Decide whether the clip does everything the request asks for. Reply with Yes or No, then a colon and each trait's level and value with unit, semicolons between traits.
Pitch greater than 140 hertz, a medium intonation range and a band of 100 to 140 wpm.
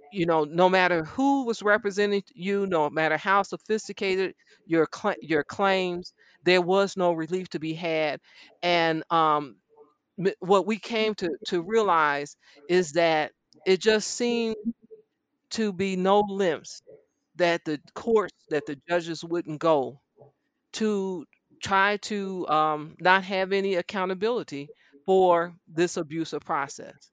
Yes: medium, 185 Hz; average, 3.8 semitones; slow, 135 wpm